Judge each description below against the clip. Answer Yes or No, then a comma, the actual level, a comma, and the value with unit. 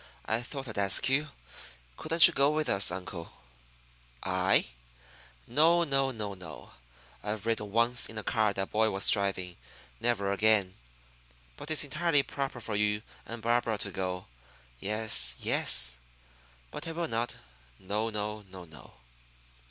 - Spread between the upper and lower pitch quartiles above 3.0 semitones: Yes, average, 5.1 semitones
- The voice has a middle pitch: No, low, 110 Hz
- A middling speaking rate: Yes, average, 145 wpm